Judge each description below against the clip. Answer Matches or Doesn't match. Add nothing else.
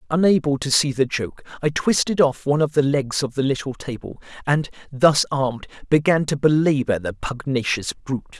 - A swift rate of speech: Doesn't match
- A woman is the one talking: Doesn't match